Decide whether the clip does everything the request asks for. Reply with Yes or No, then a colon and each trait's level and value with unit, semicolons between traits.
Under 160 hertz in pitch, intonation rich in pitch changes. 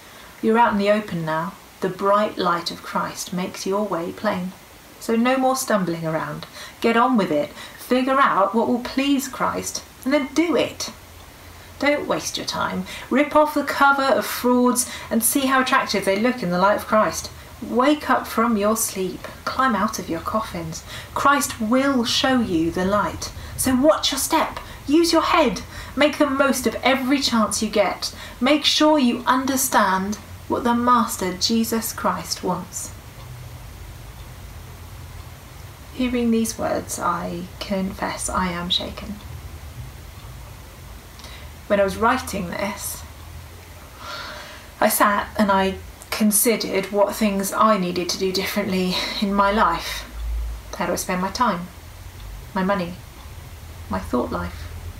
No: high, 200 Hz; wide, 7.1 semitones